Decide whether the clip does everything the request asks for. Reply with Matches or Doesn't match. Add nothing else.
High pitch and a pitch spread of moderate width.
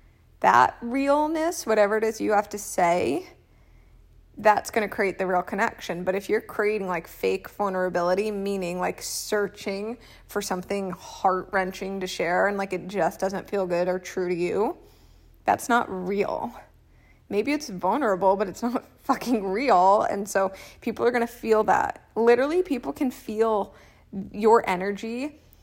Matches